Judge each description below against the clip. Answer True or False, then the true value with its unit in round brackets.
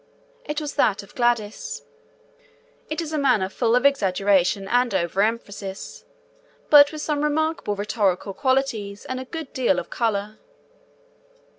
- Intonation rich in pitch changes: True (5.9 semitones)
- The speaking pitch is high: True (235 Hz)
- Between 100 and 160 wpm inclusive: True (135 wpm)